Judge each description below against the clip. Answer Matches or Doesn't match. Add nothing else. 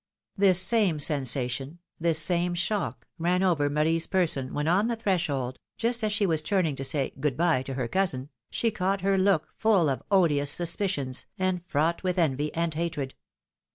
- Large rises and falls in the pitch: Doesn't match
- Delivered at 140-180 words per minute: Matches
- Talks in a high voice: Doesn't match